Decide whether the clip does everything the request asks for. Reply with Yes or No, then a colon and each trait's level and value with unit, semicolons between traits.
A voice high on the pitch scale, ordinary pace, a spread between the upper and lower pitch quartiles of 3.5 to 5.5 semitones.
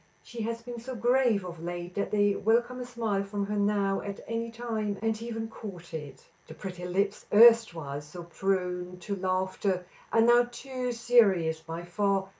Yes: high, 200 Hz; average, 175 wpm; average, 4.3 semitones